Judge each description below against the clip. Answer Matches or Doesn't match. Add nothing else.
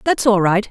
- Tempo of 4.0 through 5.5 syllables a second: Matches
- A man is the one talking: Doesn't match